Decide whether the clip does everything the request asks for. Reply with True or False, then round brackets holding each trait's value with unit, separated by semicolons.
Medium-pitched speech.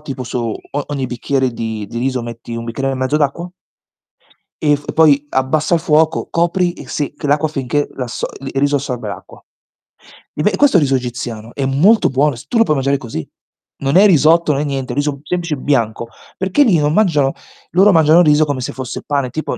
True (145 Hz)